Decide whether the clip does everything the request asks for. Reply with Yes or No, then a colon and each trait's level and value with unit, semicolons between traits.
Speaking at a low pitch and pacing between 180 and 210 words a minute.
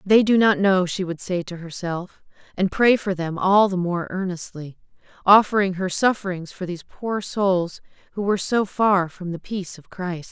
No: medium, 185 Hz; average, 190 wpm